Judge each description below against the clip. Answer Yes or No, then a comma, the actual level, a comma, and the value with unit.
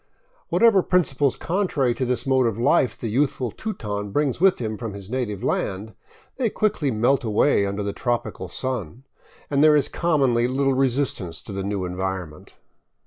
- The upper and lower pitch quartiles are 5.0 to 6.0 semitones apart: Yes, wide, 5.5 semitones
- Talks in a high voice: No, low, 125 Hz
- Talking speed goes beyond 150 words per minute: Yes, average, 170 wpm